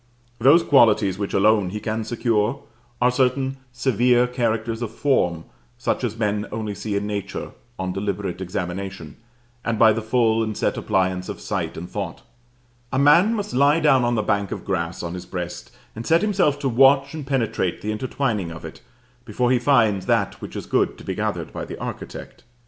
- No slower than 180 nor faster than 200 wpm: Yes, average, 190 wpm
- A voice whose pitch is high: No, low, 110 Hz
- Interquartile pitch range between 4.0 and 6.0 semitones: Yes, average, 4.7 semitones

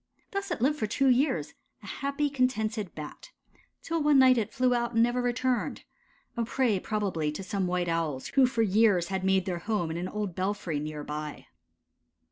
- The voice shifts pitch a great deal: Yes, wide, 6.1 semitones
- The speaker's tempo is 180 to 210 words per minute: Yes, average, 190 wpm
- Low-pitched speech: No, high, 215 Hz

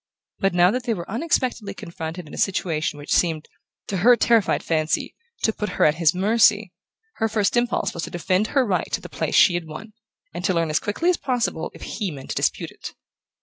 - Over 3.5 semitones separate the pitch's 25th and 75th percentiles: Yes, average, 5.2 semitones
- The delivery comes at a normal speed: No, fast, 220 wpm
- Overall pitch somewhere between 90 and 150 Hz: No, high, 190 Hz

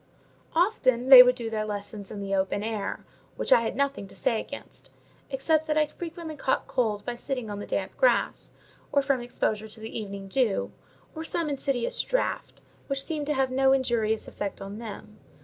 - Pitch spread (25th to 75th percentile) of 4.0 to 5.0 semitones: Yes, average, 4.7 semitones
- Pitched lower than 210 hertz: No, high, 245 Hz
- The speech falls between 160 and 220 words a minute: Yes, average, 190 wpm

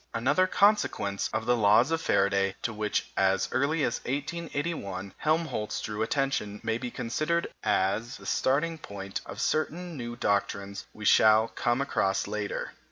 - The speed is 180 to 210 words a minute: No, average, 150 wpm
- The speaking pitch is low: Yes, low, 115 Hz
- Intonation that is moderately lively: No, wide, 6.4 semitones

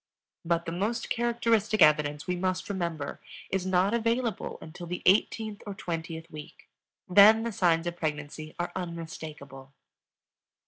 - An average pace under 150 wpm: Yes, average, 140 wpm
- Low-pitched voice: No, medium, 175 Hz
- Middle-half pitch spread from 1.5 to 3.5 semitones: No, average, 4.1 semitones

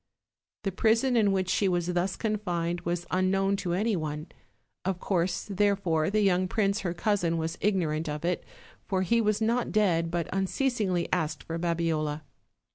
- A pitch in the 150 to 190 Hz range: Yes, medium, 185 Hz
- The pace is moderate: Yes, average, 170 wpm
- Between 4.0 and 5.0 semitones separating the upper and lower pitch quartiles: No, average, 3.3 semitones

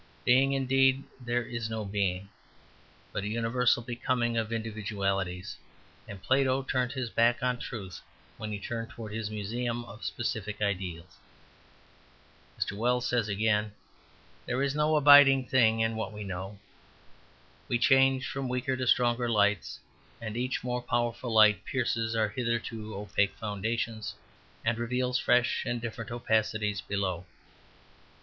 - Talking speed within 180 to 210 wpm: No, average, 140 wpm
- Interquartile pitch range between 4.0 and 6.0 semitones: No, average, 2.9 semitones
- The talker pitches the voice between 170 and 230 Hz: No, low, 115 Hz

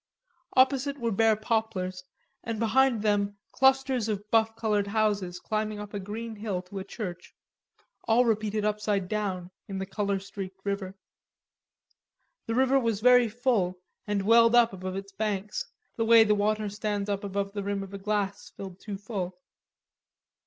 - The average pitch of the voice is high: Yes, high, 210 Hz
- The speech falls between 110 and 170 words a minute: Yes, average, 160 wpm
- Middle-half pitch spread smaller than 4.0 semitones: Yes, narrow, 2.4 semitones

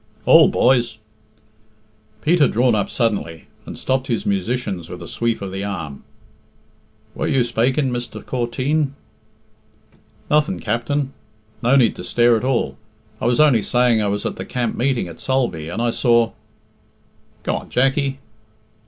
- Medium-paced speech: Yes, average, 155 wpm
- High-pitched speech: No, low, 120 Hz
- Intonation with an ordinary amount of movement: Yes, average, 3.4 semitones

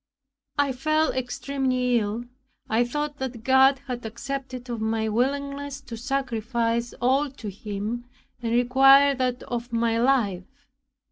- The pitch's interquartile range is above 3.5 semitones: No, average, 2.8 semitones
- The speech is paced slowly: Yes, slow, 130 wpm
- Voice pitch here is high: Yes, very high, 250 Hz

